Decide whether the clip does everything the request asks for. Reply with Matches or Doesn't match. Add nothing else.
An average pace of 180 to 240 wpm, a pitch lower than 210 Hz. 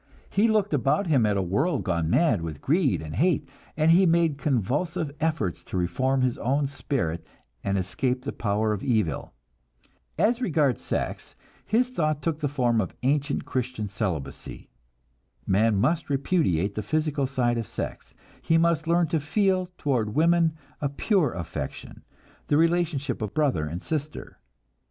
Doesn't match